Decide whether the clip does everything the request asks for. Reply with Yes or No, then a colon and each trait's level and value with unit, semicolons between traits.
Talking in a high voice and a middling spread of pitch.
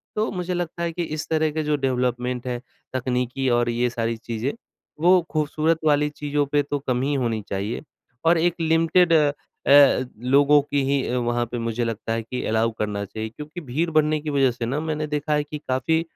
No: medium, 140 Hz; average, 4.1 semitones